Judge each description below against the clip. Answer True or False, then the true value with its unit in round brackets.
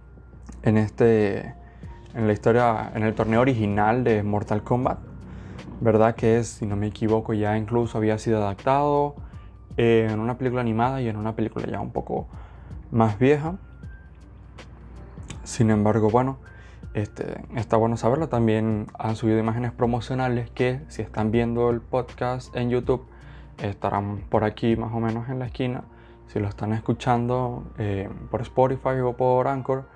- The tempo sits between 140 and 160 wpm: True (155 wpm)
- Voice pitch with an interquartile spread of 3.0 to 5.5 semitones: False (2.5 semitones)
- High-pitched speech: False (115 Hz)